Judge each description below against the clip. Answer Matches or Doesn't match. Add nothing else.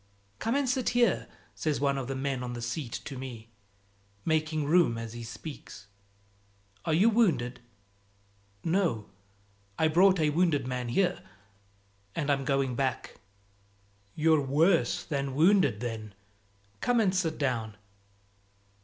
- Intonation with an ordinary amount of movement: Doesn't match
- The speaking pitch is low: Doesn't match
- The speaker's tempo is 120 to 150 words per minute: Matches